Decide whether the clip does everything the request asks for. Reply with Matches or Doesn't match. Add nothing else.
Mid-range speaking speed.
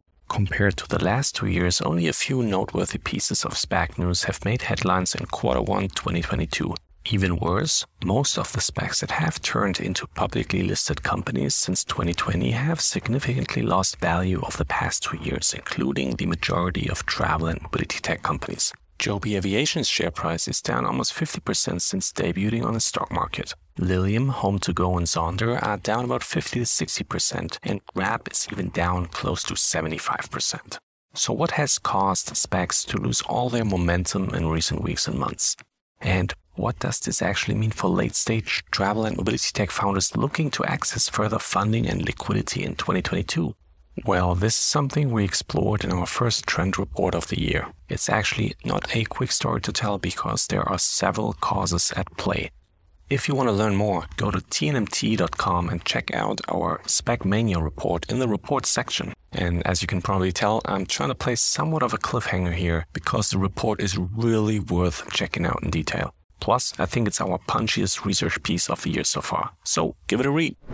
Matches